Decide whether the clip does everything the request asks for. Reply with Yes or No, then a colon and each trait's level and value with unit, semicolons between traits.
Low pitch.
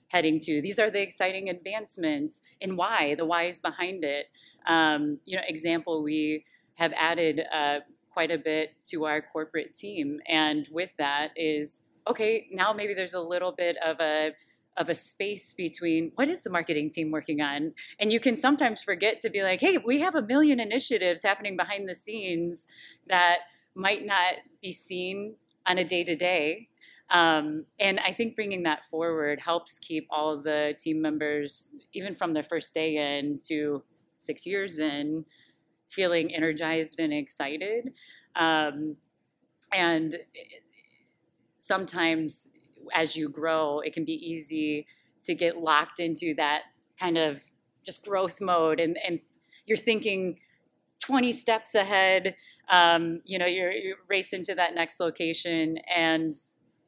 No: medium, 170 Hz